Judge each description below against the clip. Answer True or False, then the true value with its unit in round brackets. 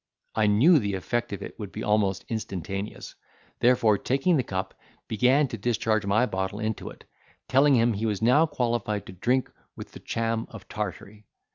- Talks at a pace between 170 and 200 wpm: True (175 wpm)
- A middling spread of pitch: True (3.3 semitones)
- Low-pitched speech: True (110 Hz)